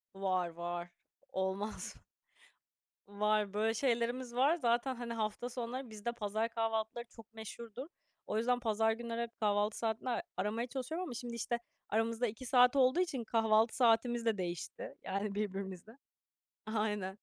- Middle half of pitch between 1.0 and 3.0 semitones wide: Yes, narrow, 2.4 semitones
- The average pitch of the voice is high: Yes, high, 225 Hz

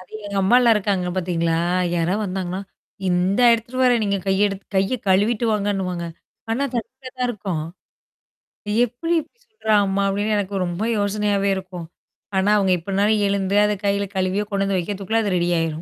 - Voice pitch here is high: Yes, high, 200 Hz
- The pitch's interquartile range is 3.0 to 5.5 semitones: No, narrow, 2.4 semitones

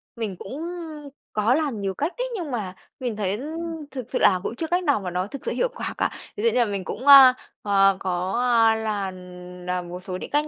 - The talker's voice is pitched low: No, high, 220 Hz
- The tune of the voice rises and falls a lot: Yes, wide, 6.2 semitones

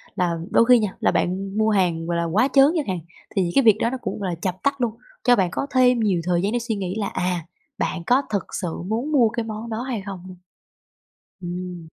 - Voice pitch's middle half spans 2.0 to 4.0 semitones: No, average, 4.6 semitones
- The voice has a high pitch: Yes, high, 200 Hz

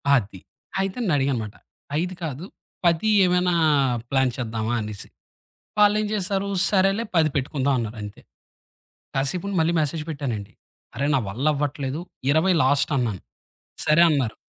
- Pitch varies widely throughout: Yes, wide, 5.9 semitones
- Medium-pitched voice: Yes, medium, 145 Hz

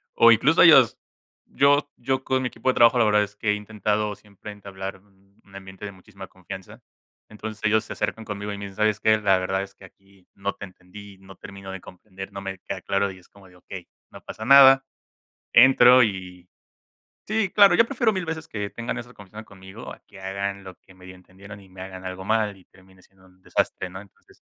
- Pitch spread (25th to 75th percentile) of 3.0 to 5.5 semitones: No, narrow, 2.6 semitones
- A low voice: Yes, low, 100 Hz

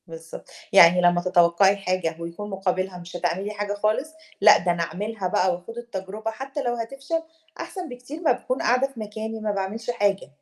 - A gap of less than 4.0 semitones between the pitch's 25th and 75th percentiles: No, average, 4.7 semitones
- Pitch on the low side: No, high, 205 Hz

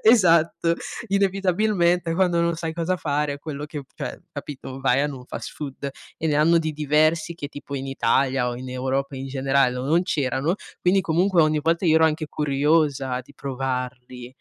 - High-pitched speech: No, medium, 150 Hz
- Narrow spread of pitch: No, average, 3.8 semitones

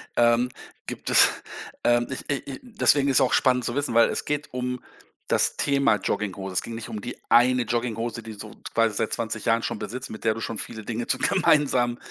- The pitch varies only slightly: Yes, narrow, 2.3 semitones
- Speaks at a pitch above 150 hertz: No, low, 120 Hz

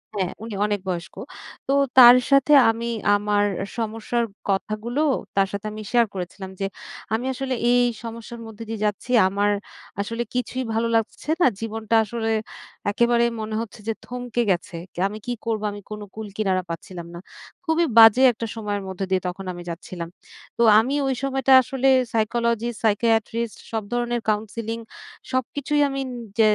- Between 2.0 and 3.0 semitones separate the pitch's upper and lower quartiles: Yes, average, 2.7 semitones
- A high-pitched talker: Yes, high, 225 Hz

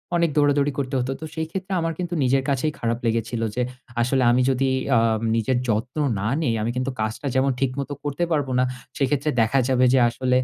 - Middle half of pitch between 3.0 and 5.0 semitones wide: Yes, average, 3.4 semitones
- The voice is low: Yes, low, 130 Hz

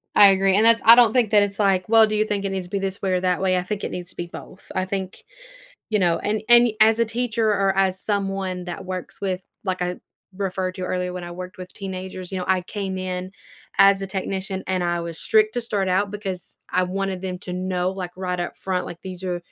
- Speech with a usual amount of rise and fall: No, narrow, 1.8 semitones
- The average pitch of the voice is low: No, high, 190 Hz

